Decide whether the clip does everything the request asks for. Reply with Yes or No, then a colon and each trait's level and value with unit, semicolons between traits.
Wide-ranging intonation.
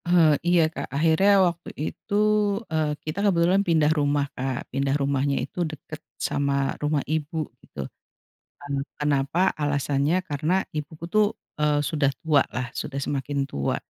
No: narrow, 2.6 semitones